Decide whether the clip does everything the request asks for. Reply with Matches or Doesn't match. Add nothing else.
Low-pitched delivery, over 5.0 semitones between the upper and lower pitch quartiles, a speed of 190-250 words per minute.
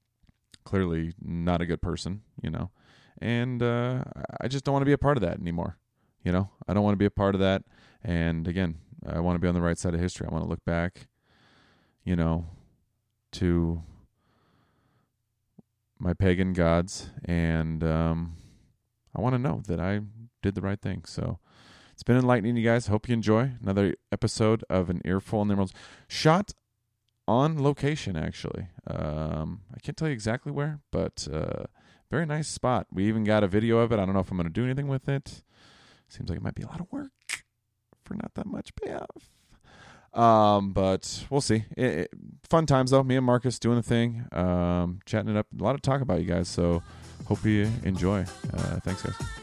Matches